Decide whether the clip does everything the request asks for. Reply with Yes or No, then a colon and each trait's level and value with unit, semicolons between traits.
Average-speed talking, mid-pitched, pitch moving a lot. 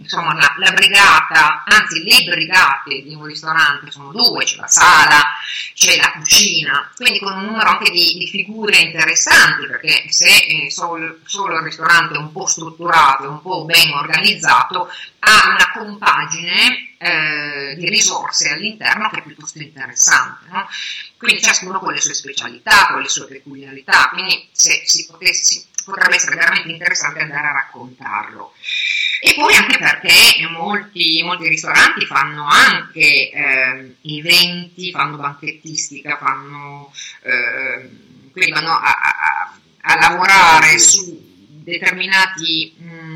No: average, 140 wpm; medium, 165 Hz; average, 3.6 semitones